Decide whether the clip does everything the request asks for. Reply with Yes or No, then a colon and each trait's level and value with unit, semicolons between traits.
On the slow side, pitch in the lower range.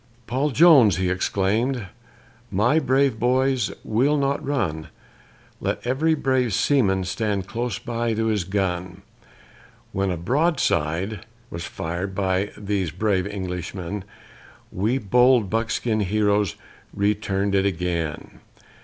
Yes: slow, 110 wpm; low, 105 Hz